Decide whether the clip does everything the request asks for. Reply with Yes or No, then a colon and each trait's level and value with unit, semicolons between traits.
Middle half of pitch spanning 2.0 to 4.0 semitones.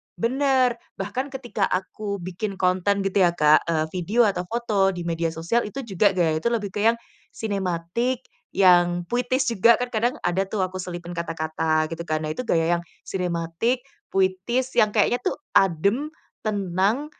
No: average, 5.1 semitones